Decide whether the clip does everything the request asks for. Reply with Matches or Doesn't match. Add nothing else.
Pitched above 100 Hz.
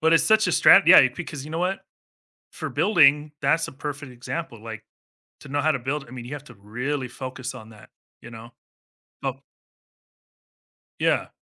Matches